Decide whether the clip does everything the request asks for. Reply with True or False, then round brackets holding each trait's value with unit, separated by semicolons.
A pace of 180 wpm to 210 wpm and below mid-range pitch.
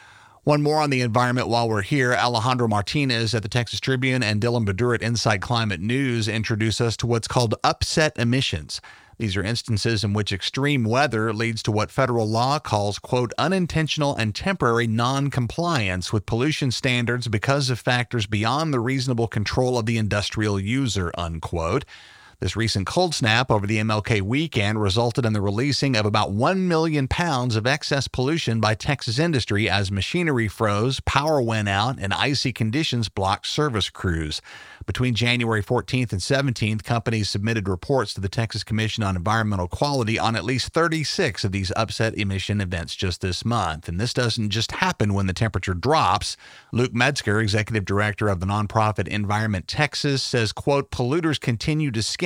False (170 wpm; 115 Hz)